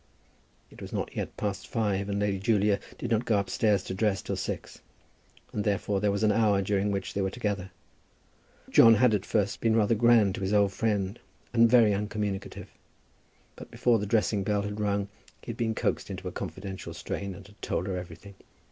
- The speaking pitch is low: Yes, low, 105 Hz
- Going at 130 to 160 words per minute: No, average, 195 wpm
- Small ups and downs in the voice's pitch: Yes, narrow, 1.7 semitones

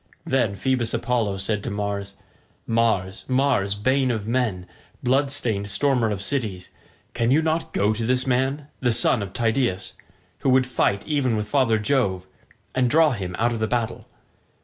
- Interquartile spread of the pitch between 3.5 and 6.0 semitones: Yes, average, 4.3 semitones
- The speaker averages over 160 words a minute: Yes, average, 170 wpm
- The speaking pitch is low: Yes, low, 115 Hz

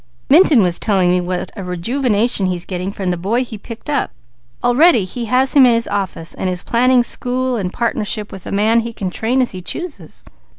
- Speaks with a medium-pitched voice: No, high, 220 Hz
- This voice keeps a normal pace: No, fast, 210 wpm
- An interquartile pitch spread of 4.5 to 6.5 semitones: Yes, average, 5.1 semitones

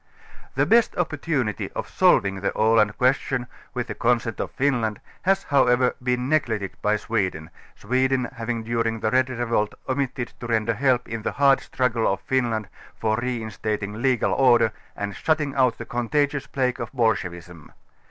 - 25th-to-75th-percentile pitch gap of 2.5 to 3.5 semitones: Yes, average, 3.1 semitones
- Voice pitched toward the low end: Yes, low, 120 Hz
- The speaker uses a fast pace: No, average, 165 wpm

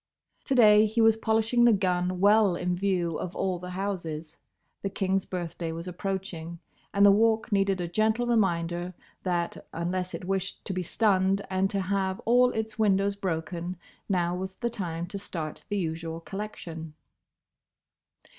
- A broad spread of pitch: No, average, 2.9 semitones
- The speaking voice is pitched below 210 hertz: Yes, high, 190 Hz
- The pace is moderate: Yes, average, 160 wpm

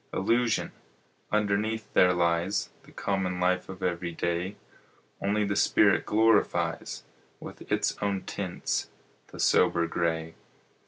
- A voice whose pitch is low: Yes, very low, 95 Hz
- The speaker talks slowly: Yes, slow, 115 wpm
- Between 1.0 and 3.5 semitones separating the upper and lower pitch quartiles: Yes, average, 3.0 semitones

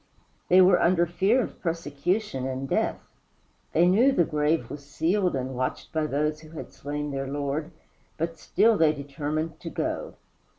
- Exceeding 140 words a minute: Yes, average, 165 wpm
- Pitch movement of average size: Yes, average, 3.6 semitones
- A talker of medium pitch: Yes, medium, 155 Hz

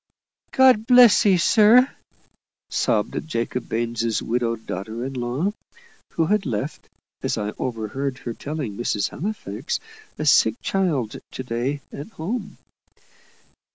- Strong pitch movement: Yes, wide, 8.8 semitones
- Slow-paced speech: Yes, slow, 120 wpm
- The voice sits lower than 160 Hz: Yes, low, 135 Hz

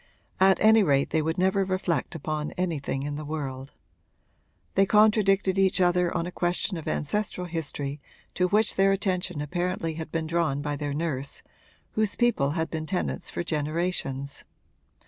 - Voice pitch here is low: No, medium, 170 Hz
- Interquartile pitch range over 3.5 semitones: Yes, average, 4.1 semitones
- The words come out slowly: No, average, 160 wpm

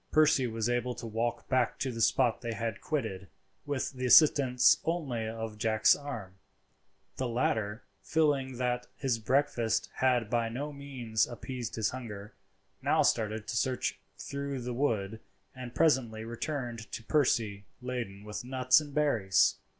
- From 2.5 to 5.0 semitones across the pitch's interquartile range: Yes, average, 3.0 semitones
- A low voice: Yes, low, 120 Hz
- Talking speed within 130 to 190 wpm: Yes, average, 150 wpm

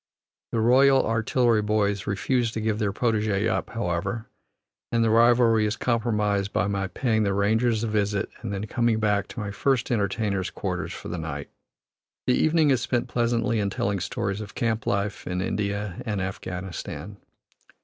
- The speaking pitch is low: Yes, low, 105 Hz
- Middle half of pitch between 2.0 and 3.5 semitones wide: Yes, narrow, 2.6 semitones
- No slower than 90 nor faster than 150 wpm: No, average, 170 wpm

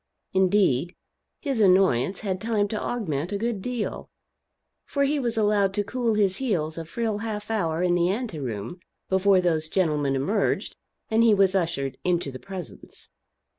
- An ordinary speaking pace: Yes, average, 165 wpm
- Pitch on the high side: Yes, high, 195 Hz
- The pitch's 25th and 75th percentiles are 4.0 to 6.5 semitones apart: Yes, average, 4.5 semitones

